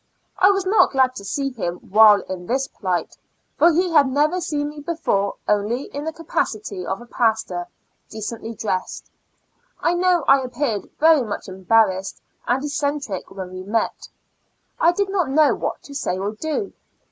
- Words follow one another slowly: No, average, 170 wpm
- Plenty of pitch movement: Yes, wide, 7.2 semitones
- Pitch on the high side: Yes, very high, 255 Hz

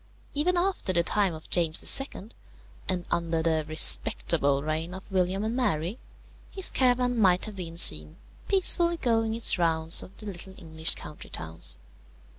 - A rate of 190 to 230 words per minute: No, average, 155 wpm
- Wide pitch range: Yes, wide, 6.1 semitones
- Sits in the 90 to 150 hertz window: No, medium, 185 Hz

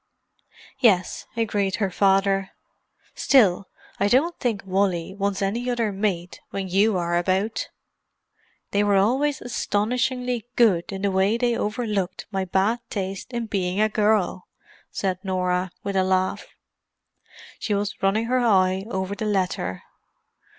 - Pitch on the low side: No, high, 200 Hz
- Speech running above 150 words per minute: No, slow, 135 wpm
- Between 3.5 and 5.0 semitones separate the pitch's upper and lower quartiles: No, average, 2.8 semitones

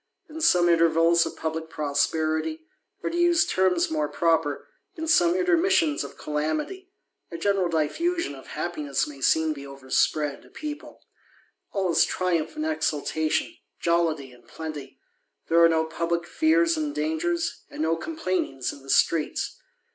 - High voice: No, medium, 165 Hz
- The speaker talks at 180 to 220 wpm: No, average, 150 wpm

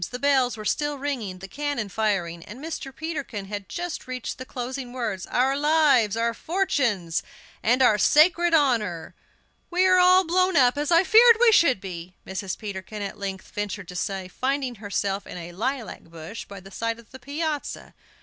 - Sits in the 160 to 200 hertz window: No, high, 245 Hz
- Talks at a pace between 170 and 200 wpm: Yes, average, 180 wpm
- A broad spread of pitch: Yes, wide, 6.8 semitones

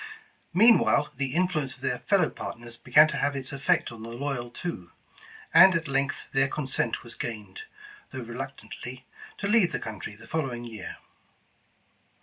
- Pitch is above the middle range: No, low, 135 Hz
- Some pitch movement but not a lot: Yes, average, 4.6 semitones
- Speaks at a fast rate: No, average, 160 wpm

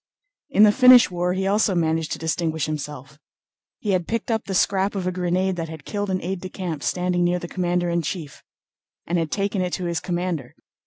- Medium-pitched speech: Yes, medium, 180 Hz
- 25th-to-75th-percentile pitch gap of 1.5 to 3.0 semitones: Yes, narrow, 2.5 semitones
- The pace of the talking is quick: Yes, fast, 215 wpm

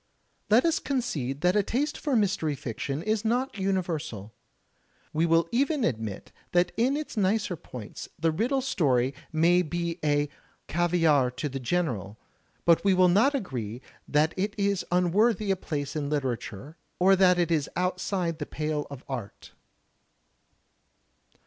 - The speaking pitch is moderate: Yes, medium, 175 Hz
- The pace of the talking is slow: No, average, 145 wpm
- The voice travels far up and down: Yes, wide, 5.8 semitones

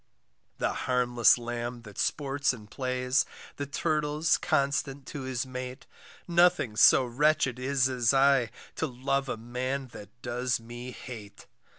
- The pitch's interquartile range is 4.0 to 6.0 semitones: No, narrow, 2.4 semitones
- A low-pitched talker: Yes, low, 130 Hz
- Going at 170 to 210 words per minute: No, slow, 135 wpm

